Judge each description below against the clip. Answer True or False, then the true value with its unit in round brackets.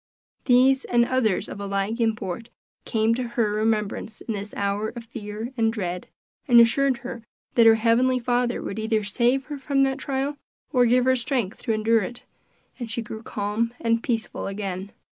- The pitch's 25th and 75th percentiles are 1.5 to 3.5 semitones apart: True (2.6 semitones)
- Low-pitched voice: False (230 Hz)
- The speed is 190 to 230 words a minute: False (180 wpm)